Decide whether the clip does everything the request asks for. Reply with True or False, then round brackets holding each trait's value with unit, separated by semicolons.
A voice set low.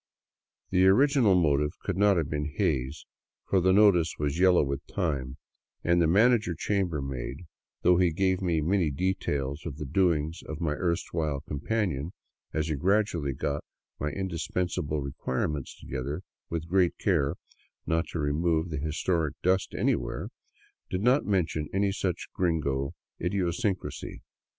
True (85 Hz)